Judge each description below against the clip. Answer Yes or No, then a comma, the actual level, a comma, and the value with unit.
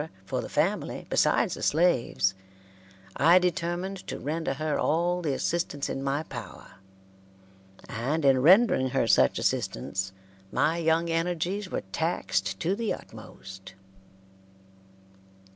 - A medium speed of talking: No, slow, 120 wpm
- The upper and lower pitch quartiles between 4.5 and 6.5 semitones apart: Yes, average, 5.2 semitones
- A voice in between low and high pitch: Yes, medium, 160 Hz